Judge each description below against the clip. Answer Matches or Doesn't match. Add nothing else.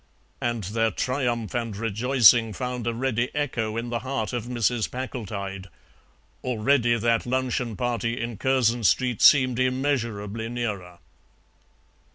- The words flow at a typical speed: Doesn't match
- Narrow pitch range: Matches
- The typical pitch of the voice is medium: Doesn't match